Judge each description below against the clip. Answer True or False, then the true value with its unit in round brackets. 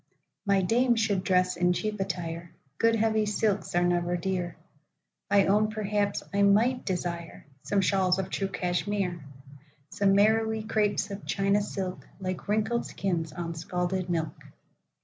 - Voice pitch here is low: False (190 Hz)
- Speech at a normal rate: False (125 wpm)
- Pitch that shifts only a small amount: False (3.0 semitones)